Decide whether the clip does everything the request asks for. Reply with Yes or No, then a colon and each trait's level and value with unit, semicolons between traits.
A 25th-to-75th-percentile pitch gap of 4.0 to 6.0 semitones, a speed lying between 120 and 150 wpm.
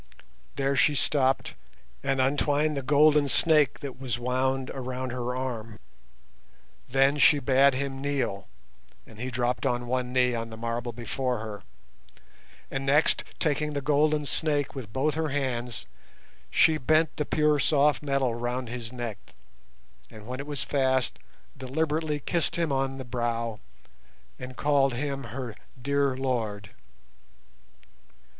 No: average, 2.7 semitones; average, 140 wpm